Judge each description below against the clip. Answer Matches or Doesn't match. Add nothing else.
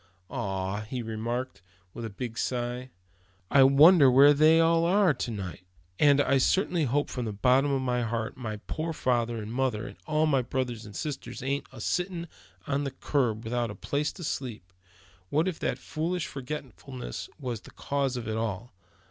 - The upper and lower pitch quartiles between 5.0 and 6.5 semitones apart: Doesn't match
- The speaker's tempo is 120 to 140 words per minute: Doesn't match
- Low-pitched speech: Matches